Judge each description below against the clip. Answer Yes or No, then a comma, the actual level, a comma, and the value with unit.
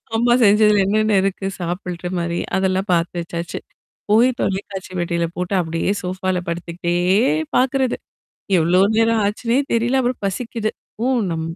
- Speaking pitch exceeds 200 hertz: No, high, 190 Hz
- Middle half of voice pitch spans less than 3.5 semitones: No, average, 4.3 semitones